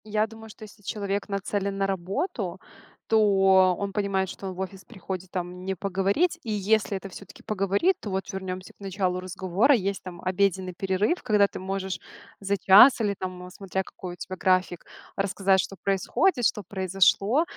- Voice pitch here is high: Yes, high, 195 Hz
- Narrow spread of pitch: Yes, narrow, 1.5 semitones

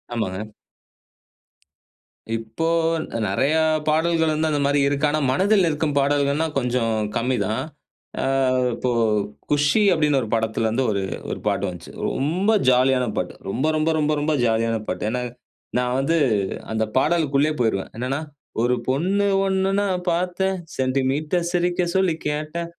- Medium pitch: Yes, medium, 145 Hz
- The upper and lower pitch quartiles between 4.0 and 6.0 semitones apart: Yes, average, 5.0 semitones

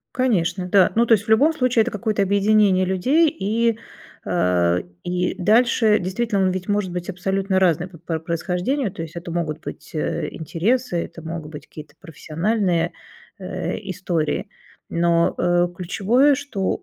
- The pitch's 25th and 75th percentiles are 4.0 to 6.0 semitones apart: Yes, average, 4.5 semitones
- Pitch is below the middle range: No, medium, 185 Hz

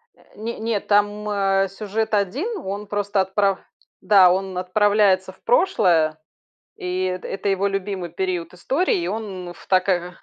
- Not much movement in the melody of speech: Yes, narrow, 2.2 semitones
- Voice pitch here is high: Yes, high, 195 Hz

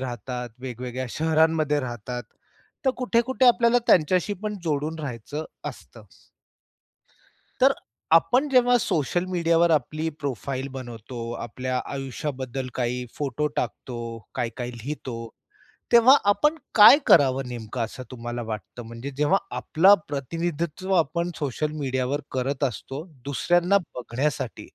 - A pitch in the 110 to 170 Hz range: Yes, medium, 140 Hz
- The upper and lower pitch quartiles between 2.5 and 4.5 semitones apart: No, average, 5.3 semitones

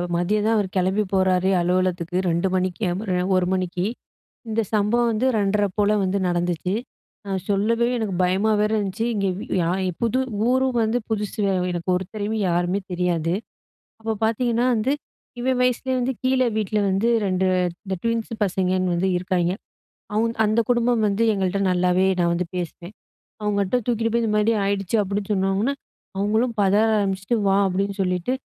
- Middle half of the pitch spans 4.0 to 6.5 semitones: No, average, 3.3 semitones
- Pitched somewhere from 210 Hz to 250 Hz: No, high, 200 Hz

